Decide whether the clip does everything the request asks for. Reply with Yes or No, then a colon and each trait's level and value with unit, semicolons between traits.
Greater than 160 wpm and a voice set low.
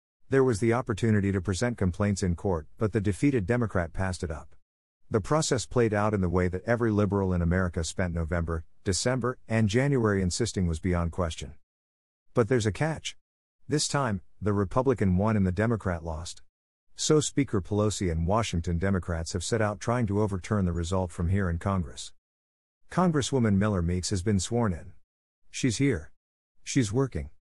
Yes: average, 170 wpm; low, 100 Hz